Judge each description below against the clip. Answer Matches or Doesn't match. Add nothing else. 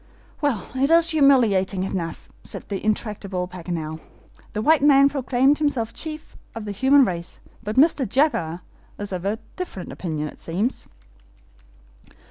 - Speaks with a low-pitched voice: Doesn't match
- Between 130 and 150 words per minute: Matches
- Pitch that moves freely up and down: Matches